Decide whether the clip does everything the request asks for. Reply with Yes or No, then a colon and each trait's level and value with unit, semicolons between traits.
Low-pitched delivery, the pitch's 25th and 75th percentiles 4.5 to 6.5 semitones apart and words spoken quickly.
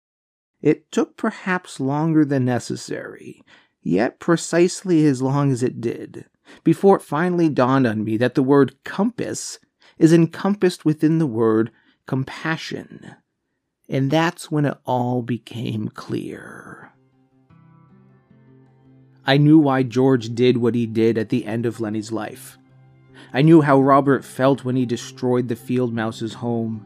No: low, 130 Hz; average, 4.8 semitones; average, 140 wpm